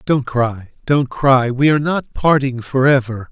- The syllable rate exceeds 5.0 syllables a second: No, 4.3 syllables/s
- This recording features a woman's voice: No, male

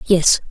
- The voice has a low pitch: No, medium, 180 Hz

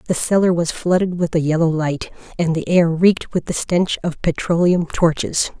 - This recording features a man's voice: No, female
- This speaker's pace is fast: No, average, 195 wpm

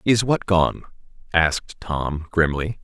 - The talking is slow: Yes, slow, 125 wpm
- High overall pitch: No, very low, 90 Hz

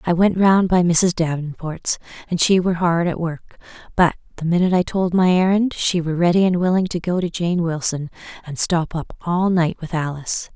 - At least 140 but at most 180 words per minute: No, fast, 205 wpm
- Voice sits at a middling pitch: Yes, medium, 175 Hz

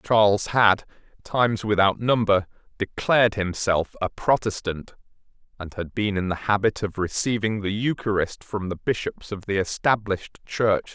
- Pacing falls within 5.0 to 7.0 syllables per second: No, 4.8 syllables/s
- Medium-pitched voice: No, low, 105 Hz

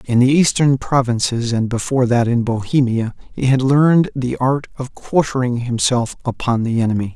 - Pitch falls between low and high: No, low, 125 Hz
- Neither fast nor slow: Yes, average, 170 wpm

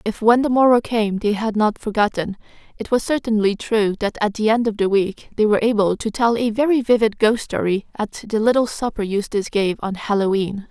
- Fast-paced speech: Yes, fast, 220 wpm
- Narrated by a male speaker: No, female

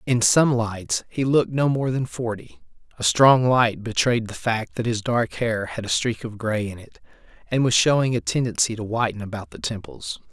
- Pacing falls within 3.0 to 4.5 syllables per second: No, 4.9 syllables/s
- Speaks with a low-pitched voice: Yes, low, 115 Hz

